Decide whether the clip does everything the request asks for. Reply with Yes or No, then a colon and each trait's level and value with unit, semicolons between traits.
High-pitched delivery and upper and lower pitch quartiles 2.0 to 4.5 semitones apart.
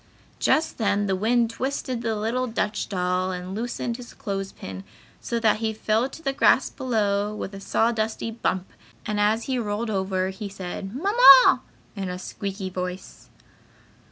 Yes: high, 215 Hz; average, 3.4 semitones